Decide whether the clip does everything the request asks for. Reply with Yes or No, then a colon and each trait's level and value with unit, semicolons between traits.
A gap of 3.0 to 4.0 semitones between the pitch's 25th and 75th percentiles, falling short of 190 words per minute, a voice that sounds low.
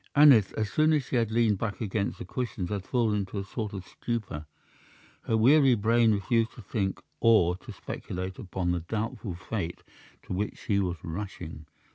Yes: average, 3.6 semitones; average, 180 wpm; low, 105 Hz